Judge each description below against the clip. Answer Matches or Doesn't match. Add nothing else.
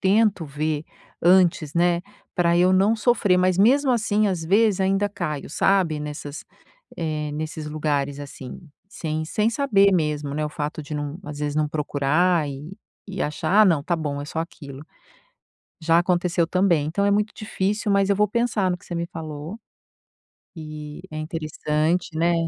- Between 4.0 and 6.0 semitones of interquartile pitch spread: Matches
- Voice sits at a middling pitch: Matches